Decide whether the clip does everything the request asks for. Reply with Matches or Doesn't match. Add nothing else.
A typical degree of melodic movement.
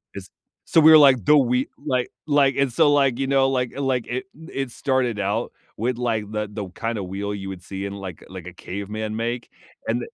Matches